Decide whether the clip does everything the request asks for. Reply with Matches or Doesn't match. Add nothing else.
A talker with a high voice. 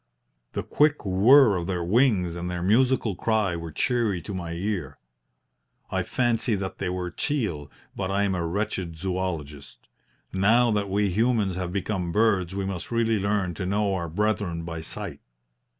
Doesn't match